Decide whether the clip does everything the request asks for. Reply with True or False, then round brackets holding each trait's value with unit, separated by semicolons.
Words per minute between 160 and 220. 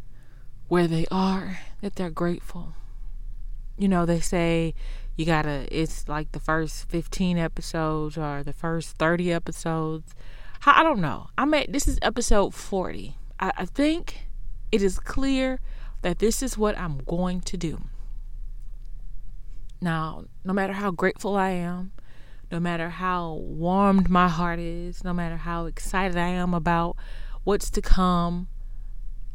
False (145 wpm)